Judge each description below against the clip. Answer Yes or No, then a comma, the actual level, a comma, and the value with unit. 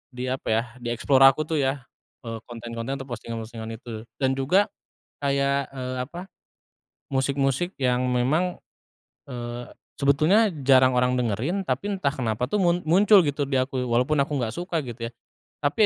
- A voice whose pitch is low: Yes, low, 130 Hz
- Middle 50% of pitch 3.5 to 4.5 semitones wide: Yes, average, 4.0 semitones